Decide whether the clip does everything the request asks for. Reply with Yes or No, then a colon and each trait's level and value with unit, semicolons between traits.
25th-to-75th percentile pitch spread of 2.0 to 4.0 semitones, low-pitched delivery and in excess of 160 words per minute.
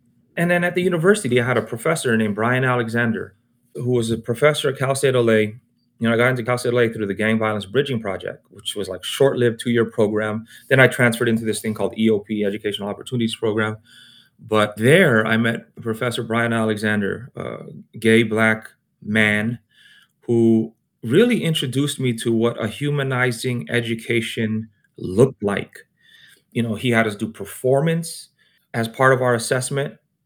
Yes: narrow, 2.5 semitones; low, 115 Hz; average, 170 wpm